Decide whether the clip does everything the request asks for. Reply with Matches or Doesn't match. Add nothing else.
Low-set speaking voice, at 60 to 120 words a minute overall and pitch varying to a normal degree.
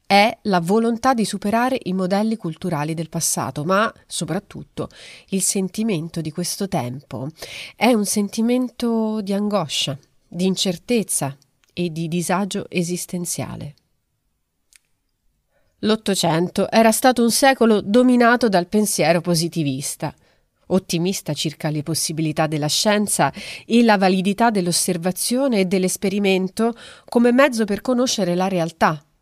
Doesn't match